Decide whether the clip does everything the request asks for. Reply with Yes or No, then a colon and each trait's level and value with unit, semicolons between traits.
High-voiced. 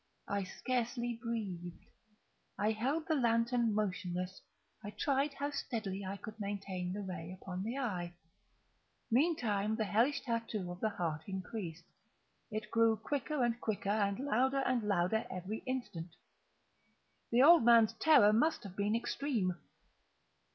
Yes: high, 220 Hz